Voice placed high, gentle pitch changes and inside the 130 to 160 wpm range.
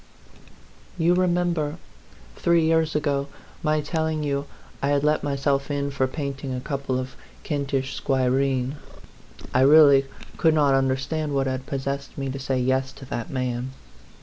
No: medium, 140 Hz; narrow, 2.3 semitones; average, 150 wpm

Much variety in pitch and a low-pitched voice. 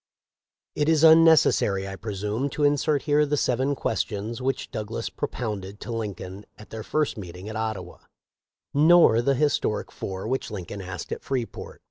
Yes: wide, 6.0 semitones; low, 115 Hz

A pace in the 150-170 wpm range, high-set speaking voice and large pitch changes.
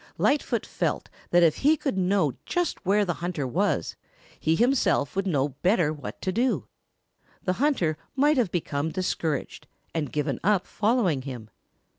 No: average, 155 wpm; medium, 180 Hz; wide, 6.9 semitones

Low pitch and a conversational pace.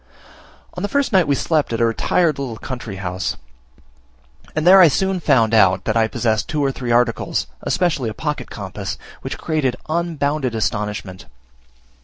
Yes: low, 130 Hz; average, 165 wpm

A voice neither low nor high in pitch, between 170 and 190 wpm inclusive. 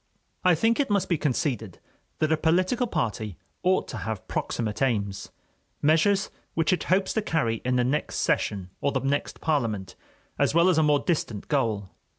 Yes: medium, 145 Hz; average, 175 wpm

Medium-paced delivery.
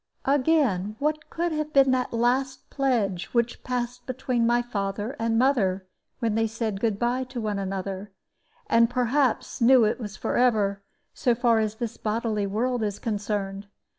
Yes: average, 165 wpm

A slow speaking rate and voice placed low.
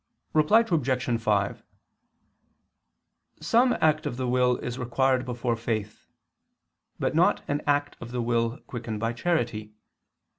Yes: slow, 125 wpm; low, 125 Hz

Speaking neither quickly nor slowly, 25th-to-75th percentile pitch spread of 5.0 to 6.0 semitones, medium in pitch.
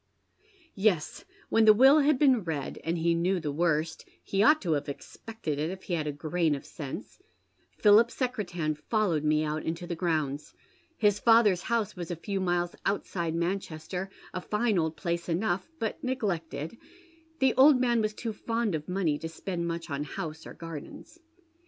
Yes: average, 185 wpm; average, 5.3 semitones; medium, 175 Hz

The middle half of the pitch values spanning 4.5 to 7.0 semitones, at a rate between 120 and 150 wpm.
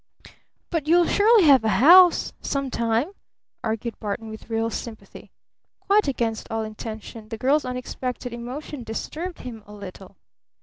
Yes: average, 5.0 semitones; average, 140 wpm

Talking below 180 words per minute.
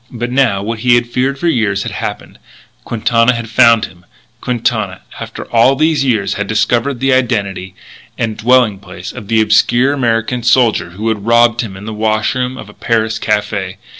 No: average, 185 wpm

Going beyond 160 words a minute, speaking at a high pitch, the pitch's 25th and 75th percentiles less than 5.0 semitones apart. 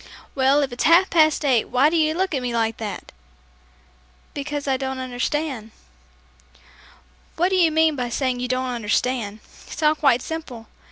Yes: average, 170 wpm; very high, 265 Hz; average, 4.1 semitones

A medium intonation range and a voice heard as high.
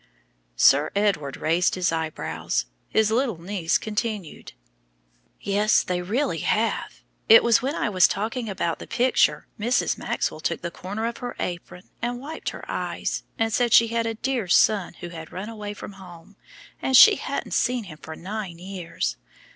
Yes: average, 4.6 semitones; high, 205 Hz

